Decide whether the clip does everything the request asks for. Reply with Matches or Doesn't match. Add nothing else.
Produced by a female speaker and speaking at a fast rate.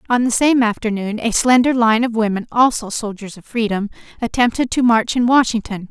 Doesn't match